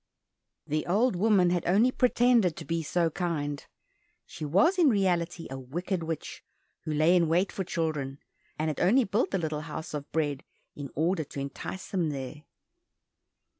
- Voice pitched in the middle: Yes, medium, 165 Hz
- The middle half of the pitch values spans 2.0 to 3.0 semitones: No, average, 4.0 semitones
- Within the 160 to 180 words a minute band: Yes, average, 170 wpm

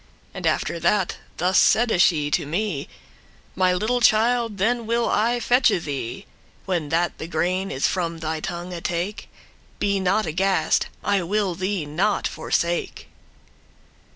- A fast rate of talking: No, average, 140 wpm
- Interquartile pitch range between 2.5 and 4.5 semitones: Yes, average, 4.0 semitones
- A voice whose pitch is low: No, medium, 185 Hz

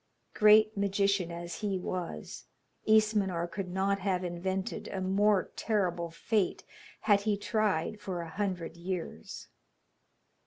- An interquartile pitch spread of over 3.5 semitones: No, average, 2.7 semitones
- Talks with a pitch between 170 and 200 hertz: Yes, high, 190 Hz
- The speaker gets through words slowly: Yes, slow, 120 wpm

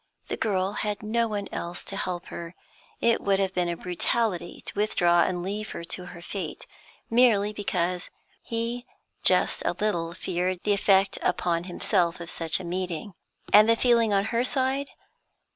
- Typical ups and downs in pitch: Yes, average, 3.5 semitones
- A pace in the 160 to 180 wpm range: Yes, average, 165 wpm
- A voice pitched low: No, high, 195 Hz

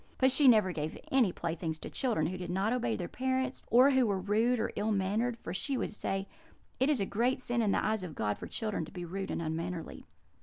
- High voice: Yes, high, 210 Hz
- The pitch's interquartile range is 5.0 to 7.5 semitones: Yes, wide, 5.4 semitones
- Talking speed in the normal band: No, fast, 240 wpm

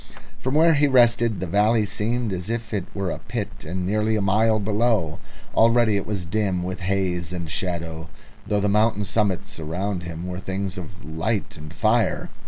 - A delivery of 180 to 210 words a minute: Yes, average, 190 wpm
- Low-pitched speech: Yes, low, 100 Hz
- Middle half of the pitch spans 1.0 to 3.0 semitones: No, average, 3.6 semitones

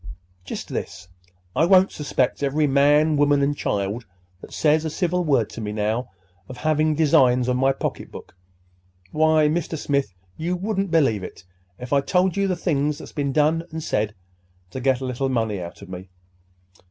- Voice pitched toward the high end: No, medium, 140 Hz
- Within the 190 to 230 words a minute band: No, average, 175 wpm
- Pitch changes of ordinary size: Yes, average, 4.3 semitones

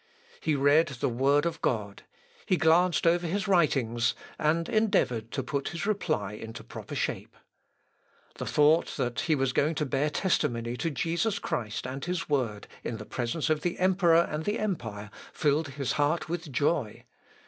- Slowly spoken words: No, average, 165 wpm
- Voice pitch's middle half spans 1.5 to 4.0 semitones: No, wide, 5.6 semitones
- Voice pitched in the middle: Yes, medium, 150 Hz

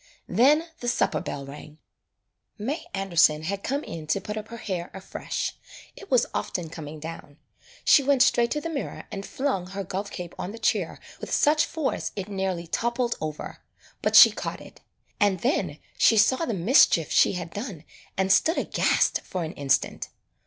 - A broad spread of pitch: Yes, wide, 6.3 semitones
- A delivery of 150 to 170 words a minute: No, average, 180 wpm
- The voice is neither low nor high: No, high, 195 Hz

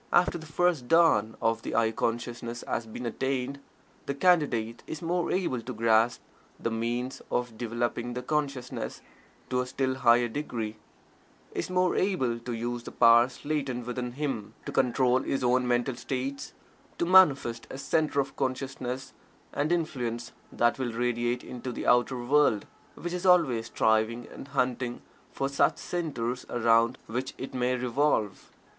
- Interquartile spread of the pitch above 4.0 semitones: No, average, 2.9 semitones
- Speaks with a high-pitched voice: No, low, 125 Hz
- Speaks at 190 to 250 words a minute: No, average, 155 wpm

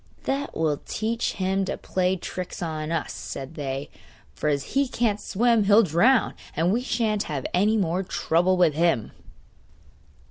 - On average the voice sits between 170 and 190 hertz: Yes, medium, 185 Hz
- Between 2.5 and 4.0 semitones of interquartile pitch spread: No, average, 5.3 semitones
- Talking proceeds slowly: No, average, 155 wpm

